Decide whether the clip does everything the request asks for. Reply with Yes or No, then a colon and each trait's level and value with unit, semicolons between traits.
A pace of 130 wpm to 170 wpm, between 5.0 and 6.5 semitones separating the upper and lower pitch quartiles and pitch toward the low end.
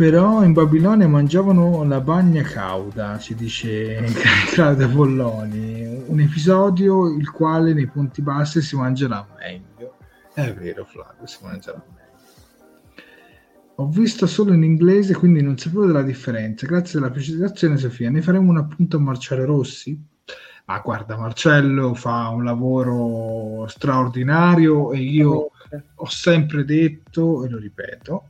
No: average, 135 wpm; wide, 5.6 semitones; medium, 145 Hz